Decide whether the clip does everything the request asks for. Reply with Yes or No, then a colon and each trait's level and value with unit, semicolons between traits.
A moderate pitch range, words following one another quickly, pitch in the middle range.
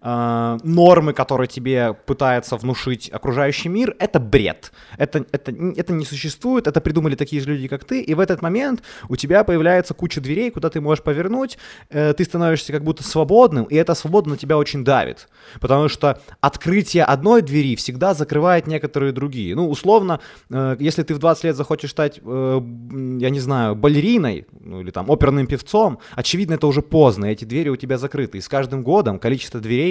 Yes: average, 4.2 semitones; fast, 185 wpm; medium, 145 Hz